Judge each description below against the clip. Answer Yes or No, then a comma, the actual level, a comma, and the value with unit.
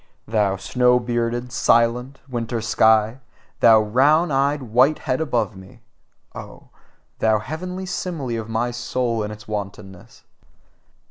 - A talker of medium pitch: No, low, 120 Hz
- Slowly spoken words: Yes, slow, 120 wpm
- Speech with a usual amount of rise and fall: Yes, average, 3.2 semitones